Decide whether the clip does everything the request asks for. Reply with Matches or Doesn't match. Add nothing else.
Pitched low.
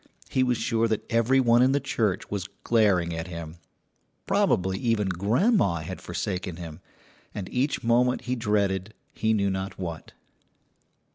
Matches